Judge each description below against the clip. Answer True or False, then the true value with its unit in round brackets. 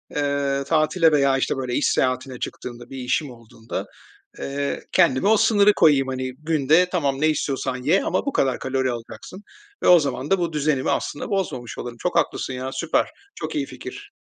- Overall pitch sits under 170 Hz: True (140 Hz)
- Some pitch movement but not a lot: True (3.9 semitones)